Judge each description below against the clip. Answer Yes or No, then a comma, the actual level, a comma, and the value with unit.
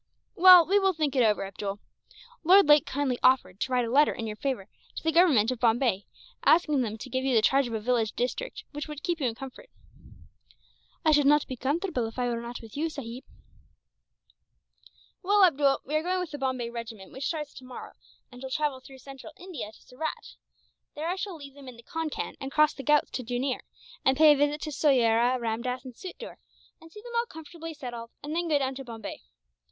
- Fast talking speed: Yes, fast, 215 wpm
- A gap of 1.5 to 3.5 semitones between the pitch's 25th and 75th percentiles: No, average, 4.3 semitones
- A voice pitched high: Yes, very high, 270 Hz